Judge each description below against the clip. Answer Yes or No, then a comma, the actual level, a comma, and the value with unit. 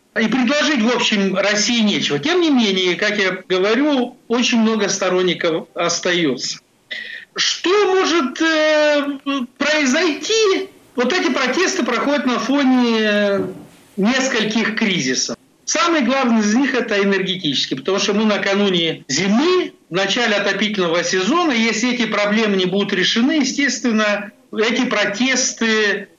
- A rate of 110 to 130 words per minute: Yes, average, 120 wpm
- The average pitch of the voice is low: No, high, 230 Hz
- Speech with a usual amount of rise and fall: No, wide, 6.0 semitones